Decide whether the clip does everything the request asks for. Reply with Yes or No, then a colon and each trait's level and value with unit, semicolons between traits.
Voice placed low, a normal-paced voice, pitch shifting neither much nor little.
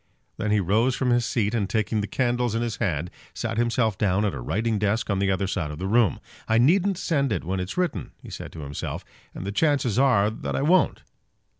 No: low, 110 Hz; fast, 235 wpm; average, 3.8 semitones